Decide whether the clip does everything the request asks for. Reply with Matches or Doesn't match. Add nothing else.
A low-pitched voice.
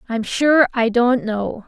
Doesn't match